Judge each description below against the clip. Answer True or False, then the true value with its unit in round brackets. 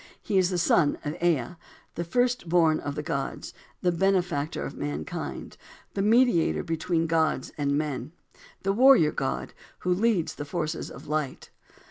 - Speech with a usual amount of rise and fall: True (3.7 semitones)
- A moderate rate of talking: True (155 wpm)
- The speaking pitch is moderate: True (165 Hz)